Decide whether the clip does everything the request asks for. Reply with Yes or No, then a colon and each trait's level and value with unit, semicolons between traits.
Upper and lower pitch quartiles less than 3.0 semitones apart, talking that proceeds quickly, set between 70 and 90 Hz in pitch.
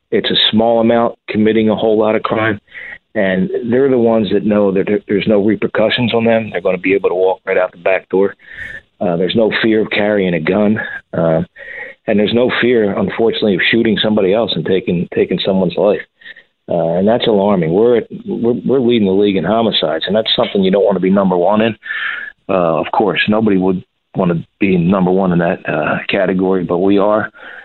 No: narrow, 2.6 semitones; fast, 215 wpm; low, 105 Hz